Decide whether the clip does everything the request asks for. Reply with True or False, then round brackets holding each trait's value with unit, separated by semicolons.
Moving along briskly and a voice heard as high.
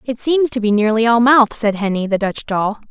True (250 wpm; 225 Hz)